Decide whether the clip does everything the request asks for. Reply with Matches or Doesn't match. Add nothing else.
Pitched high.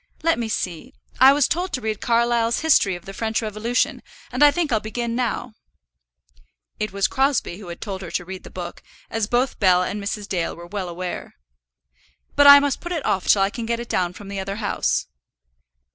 Matches